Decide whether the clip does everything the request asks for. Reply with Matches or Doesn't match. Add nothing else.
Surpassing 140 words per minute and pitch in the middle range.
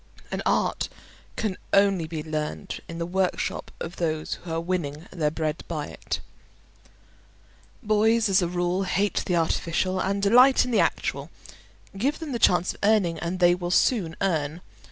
Matches